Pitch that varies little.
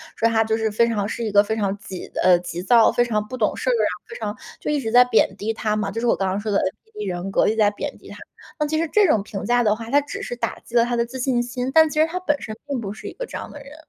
No: average, 3.6 semitones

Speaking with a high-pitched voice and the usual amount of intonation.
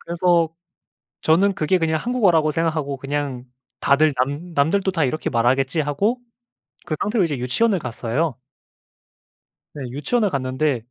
No: medium, 155 Hz; average, 4.3 semitones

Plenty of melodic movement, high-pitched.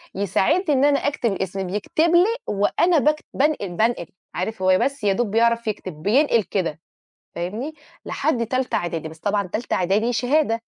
Yes: wide, 6.6 semitones; high, 225 Hz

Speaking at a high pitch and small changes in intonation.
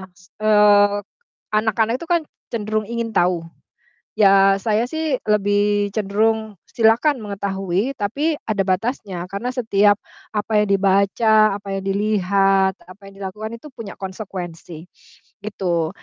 Yes: high, 205 Hz; narrow, 2.1 semitones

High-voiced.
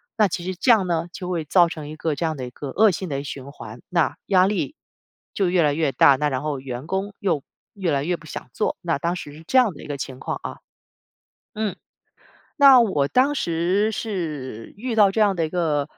No: medium, 170 Hz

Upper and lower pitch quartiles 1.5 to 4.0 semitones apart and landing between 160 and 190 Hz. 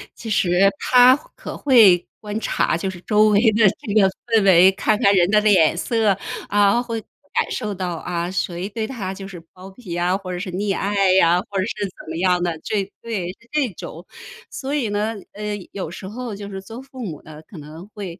No: average, 3.3 semitones; high, 200 Hz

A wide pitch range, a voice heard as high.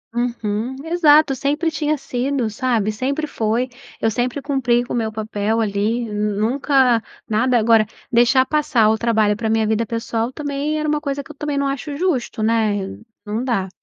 No: average, 4.3 semitones; high, 240 Hz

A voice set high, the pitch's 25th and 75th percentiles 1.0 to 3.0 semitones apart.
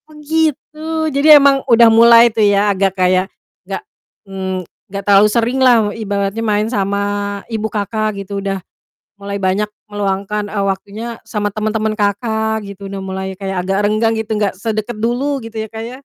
Yes: high, 210 Hz; narrow, 2.6 semitones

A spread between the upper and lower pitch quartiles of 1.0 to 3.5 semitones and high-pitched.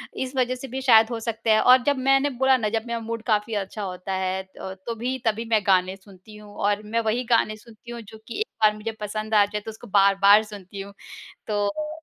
Yes: narrow, 2.6 semitones; high, 215 Hz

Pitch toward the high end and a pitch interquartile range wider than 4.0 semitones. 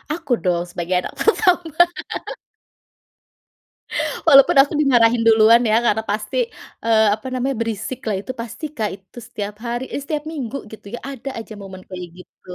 Yes: high, 230 Hz; average, 4.4 semitones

